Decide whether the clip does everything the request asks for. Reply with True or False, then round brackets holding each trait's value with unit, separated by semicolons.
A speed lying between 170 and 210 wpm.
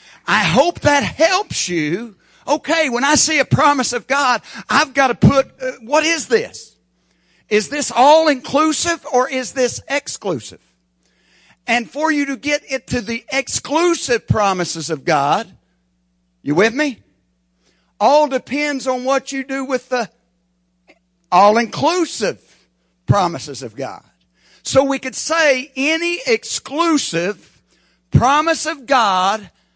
False (135 wpm)